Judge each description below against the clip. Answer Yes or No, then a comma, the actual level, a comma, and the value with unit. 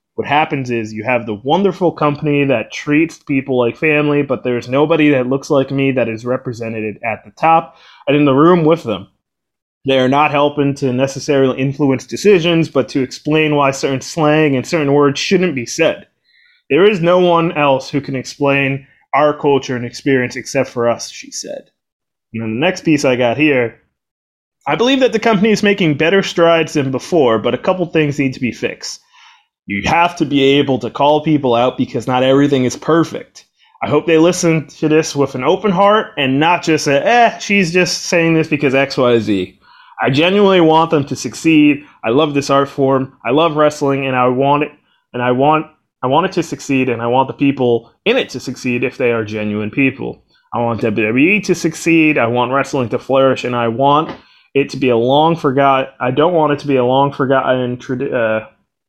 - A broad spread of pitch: No, average, 3.8 semitones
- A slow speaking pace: No, fast, 205 wpm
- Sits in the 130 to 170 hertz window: Yes, medium, 140 Hz